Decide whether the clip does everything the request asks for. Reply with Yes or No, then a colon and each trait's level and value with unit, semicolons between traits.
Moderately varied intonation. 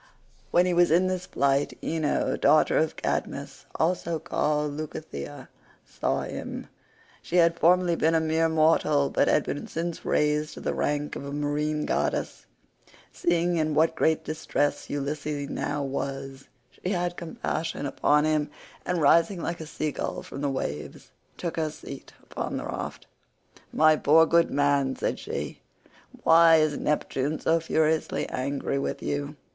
No: narrow, 2.3 semitones